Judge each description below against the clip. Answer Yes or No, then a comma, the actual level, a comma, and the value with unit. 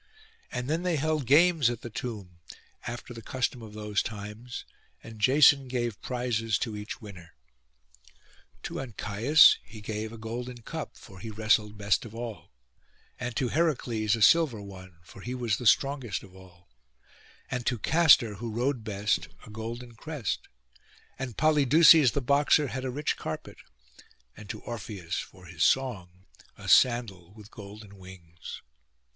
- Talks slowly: No, average, 155 wpm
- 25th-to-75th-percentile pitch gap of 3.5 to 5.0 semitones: Yes, average, 3.8 semitones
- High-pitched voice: No, low, 115 Hz